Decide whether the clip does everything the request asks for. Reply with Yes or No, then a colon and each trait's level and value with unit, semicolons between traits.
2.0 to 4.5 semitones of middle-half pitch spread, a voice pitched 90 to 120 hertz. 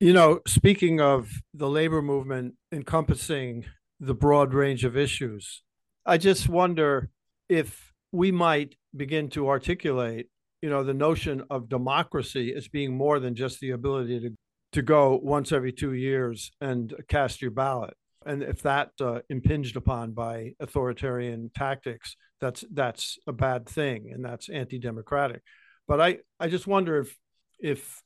No: average, 2.9 semitones; low, 135 Hz